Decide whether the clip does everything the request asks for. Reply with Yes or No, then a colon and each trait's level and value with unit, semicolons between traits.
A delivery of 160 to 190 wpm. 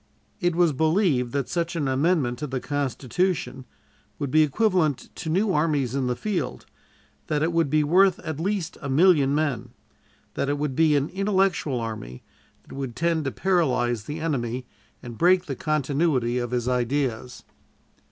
Yes: average, 165 wpm